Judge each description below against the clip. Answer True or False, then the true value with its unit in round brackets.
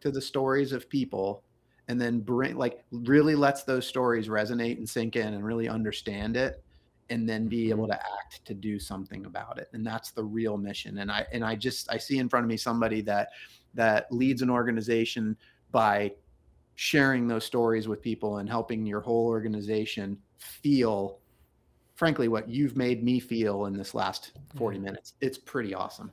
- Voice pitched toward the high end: False (115 Hz)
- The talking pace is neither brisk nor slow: True (185 wpm)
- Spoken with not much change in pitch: False (3.0 semitones)